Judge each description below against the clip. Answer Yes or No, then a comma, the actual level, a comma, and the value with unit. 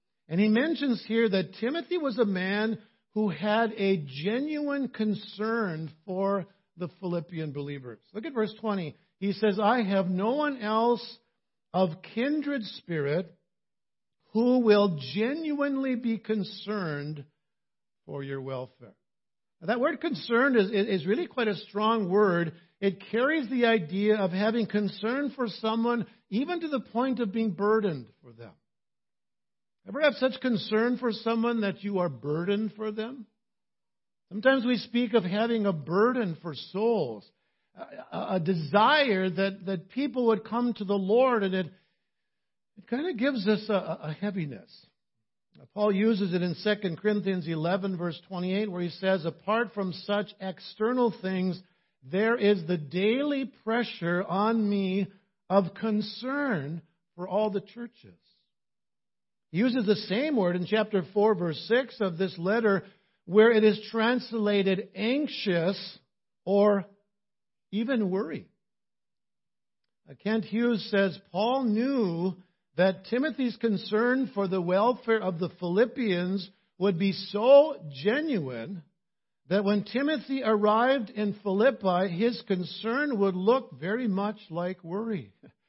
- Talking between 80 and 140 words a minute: Yes, slow, 135 wpm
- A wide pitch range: No, average, 3.6 semitones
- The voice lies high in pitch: Yes, high, 205 Hz